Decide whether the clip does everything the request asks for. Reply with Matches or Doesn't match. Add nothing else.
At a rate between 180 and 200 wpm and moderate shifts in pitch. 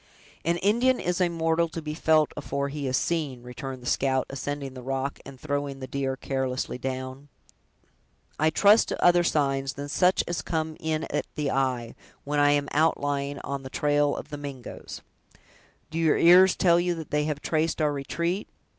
Matches